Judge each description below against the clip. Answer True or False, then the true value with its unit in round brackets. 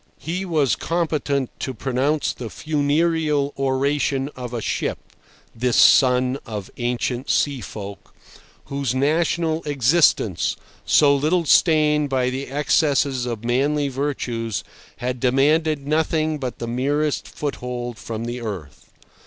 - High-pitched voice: False (140 Hz)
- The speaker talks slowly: True (120 wpm)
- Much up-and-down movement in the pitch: False (3.4 semitones)